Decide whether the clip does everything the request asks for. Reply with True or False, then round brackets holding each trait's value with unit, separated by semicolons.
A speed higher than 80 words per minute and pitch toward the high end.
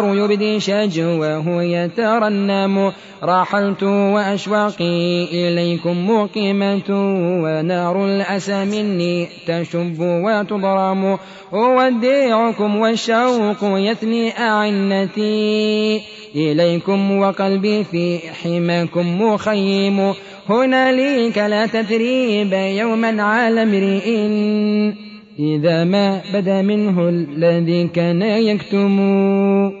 False (70 wpm; 200 Hz)